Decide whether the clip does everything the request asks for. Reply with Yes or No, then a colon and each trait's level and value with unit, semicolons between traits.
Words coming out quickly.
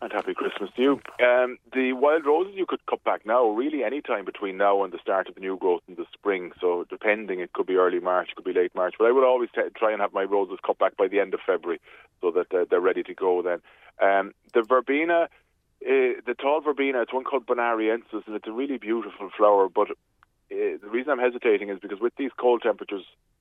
Yes: fast, 245 wpm